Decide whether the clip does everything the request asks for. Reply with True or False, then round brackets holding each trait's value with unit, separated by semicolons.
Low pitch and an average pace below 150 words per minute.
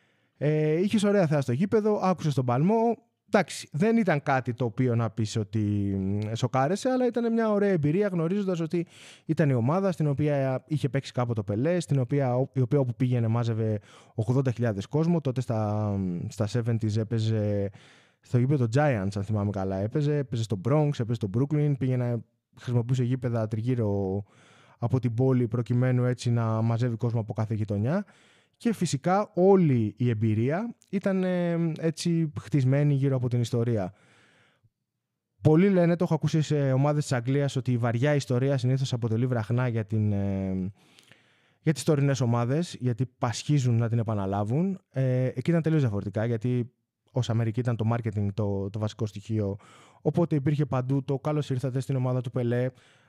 False (125 Hz; 165 wpm)